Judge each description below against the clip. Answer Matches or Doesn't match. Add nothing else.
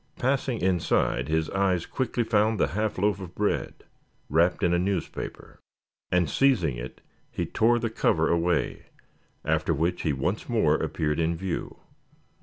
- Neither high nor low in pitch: Doesn't match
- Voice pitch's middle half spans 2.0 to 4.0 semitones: Doesn't match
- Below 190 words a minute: Matches